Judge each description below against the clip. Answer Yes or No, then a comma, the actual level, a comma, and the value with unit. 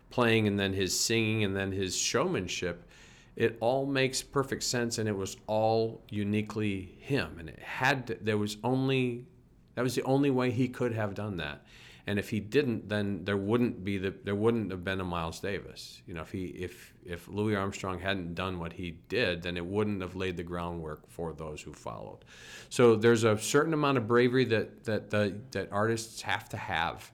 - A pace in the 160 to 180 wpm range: No, fast, 205 wpm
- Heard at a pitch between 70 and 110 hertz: Yes, low, 105 Hz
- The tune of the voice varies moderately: Yes, average, 3.9 semitones